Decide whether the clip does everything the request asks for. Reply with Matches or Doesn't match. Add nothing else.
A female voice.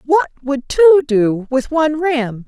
Matches